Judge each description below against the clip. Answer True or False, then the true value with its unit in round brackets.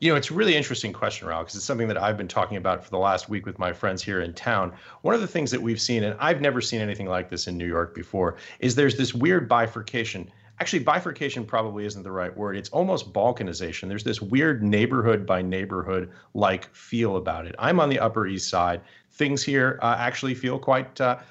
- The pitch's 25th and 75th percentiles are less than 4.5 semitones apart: False (5.6 semitones)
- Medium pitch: False (110 Hz)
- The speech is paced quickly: True (230 wpm)